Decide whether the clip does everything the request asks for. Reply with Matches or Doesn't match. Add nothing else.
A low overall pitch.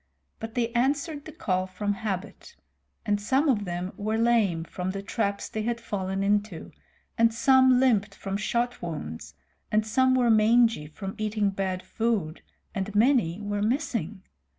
Doesn't match